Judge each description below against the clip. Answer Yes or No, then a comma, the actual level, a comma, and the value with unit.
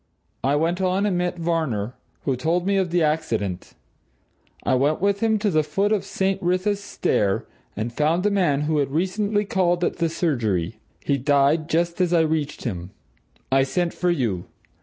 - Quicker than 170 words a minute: Yes, average, 180 wpm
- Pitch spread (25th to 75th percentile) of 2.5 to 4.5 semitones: No, average, 4.9 semitones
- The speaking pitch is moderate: Yes, medium, 165 Hz